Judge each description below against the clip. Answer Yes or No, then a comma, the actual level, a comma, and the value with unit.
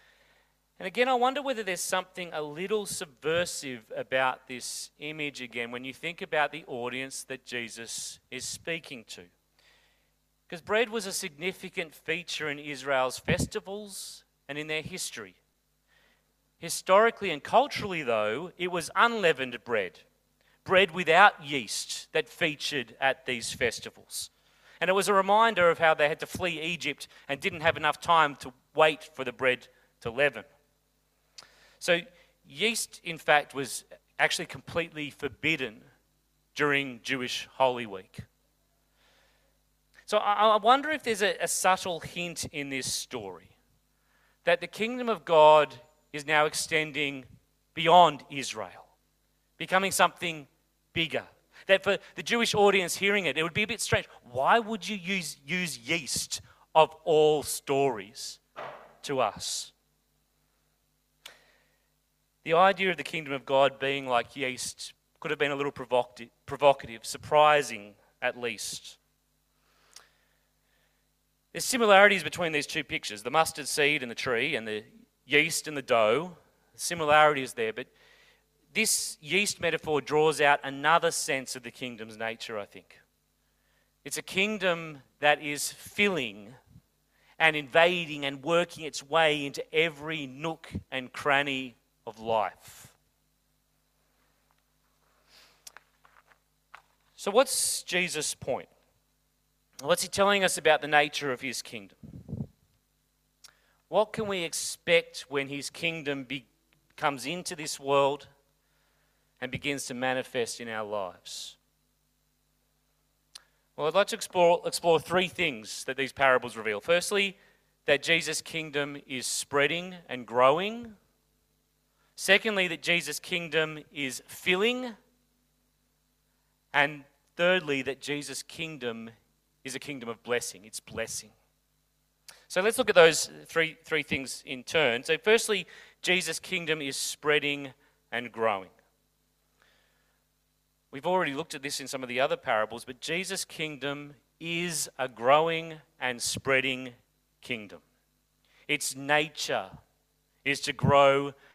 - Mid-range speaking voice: Yes, medium, 150 Hz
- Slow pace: Yes, slow, 130 wpm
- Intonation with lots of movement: No, average, 4.9 semitones